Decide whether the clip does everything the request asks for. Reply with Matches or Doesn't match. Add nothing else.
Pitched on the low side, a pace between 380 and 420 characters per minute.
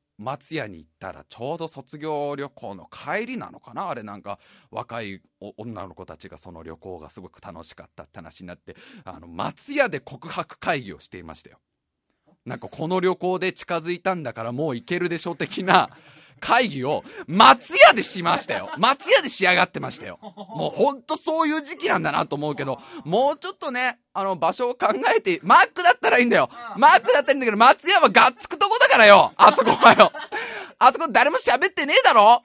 Doesn't match